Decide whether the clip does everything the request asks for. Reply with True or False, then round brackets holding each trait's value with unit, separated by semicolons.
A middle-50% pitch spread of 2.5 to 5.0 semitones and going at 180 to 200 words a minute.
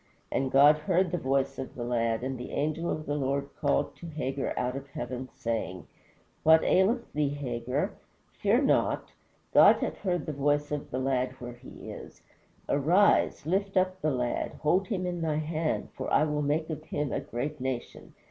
True (3.5 semitones; 185 wpm)